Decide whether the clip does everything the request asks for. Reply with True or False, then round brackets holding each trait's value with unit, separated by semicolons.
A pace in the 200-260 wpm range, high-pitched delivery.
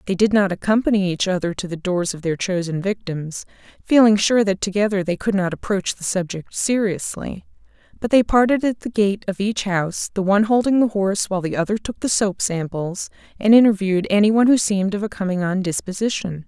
True (205 wpm; 200 Hz)